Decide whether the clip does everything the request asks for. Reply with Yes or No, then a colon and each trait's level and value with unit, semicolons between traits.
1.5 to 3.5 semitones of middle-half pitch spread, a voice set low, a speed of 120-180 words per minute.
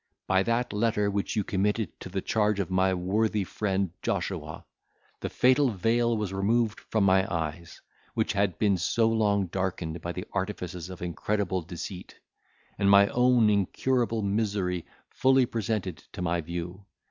Yes: average, 3.2 semitones; low, 100 Hz; average, 155 wpm